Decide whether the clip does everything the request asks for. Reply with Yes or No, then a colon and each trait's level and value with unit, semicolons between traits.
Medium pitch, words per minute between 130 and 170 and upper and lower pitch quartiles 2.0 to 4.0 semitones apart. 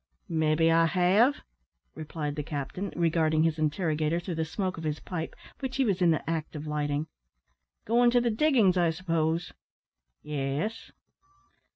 Yes: medium, 165 Hz; average, 155 wpm; average, 3.3 semitones